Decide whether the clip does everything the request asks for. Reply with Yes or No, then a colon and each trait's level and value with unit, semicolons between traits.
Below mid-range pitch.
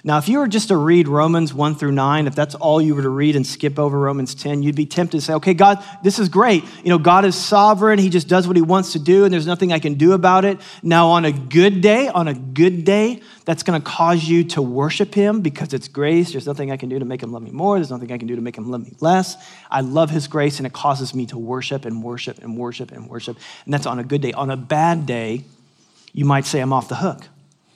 No: medium, 155 Hz